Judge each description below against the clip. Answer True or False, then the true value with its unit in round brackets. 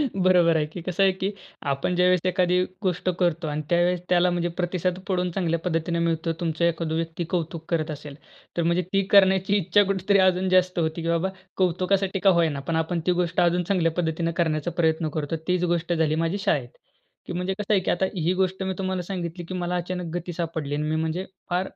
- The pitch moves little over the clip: True (1.9 semitones)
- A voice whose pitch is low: False (175 Hz)